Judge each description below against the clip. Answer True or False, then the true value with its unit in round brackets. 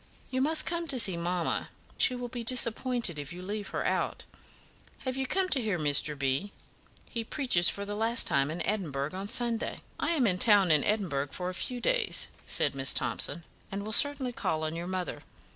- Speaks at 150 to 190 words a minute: False (205 wpm)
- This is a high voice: True (205 Hz)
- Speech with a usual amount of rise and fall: False (6.6 semitones)